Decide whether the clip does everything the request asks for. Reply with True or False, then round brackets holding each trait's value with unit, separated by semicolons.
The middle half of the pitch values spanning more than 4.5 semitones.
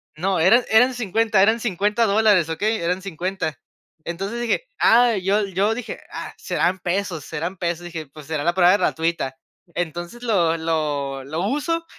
True (5.0 semitones)